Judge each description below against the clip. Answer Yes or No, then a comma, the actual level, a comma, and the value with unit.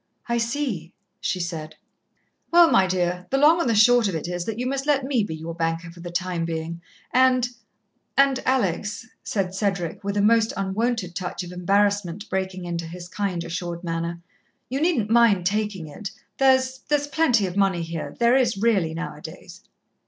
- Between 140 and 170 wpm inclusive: No, average, 185 wpm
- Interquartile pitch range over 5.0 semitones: Yes, wide, 5.6 semitones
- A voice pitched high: Yes, high, 195 Hz